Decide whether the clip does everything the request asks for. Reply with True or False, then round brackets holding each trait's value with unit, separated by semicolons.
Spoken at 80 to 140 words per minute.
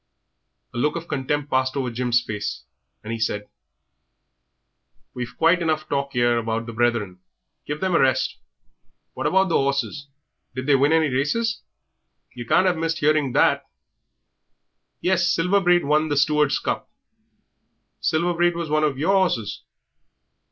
False (150 wpm)